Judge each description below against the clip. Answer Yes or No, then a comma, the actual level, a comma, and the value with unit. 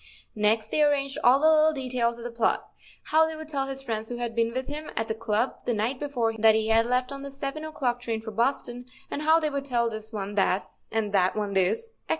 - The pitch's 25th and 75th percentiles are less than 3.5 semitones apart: No, average, 4.0 semitones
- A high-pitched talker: Yes, high, 240 Hz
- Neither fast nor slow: No, fast, 245 wpm